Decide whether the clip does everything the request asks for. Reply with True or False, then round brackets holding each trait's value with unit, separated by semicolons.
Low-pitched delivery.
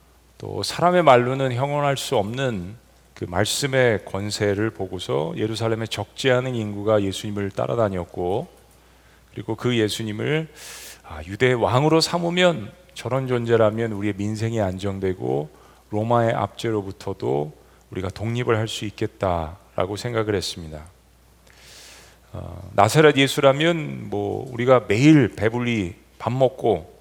True (110 Hz)